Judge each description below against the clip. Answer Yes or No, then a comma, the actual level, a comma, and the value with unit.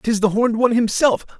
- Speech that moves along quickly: Yes, fast, 215 wpm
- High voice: Yes, high, 230 Hz